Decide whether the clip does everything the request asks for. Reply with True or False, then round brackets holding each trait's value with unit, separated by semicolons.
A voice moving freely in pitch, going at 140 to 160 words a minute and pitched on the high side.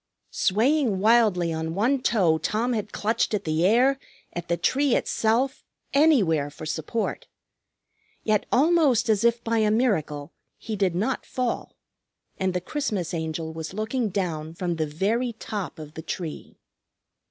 True (6.2 semitones; 150 wpm; 210 Hz)